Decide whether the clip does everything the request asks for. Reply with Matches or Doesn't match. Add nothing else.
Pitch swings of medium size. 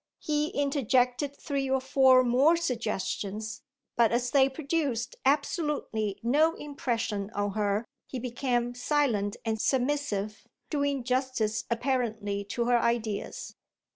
Matches